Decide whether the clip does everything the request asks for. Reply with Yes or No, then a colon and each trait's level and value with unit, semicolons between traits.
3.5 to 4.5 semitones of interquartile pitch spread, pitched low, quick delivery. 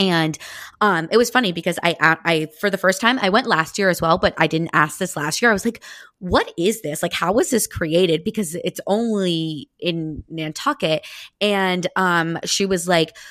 No: average, 3.8 semitones; medium, 180 Hz; fast, 210 wpm